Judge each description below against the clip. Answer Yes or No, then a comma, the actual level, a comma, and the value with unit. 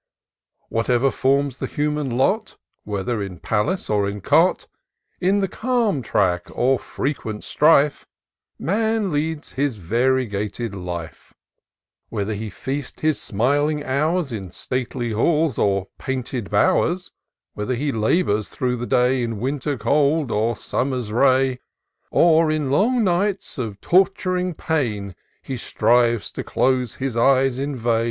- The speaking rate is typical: No, slow, 130 wpm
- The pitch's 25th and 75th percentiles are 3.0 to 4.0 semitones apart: No, average, 5.3 semitones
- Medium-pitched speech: No, low, 130 Hz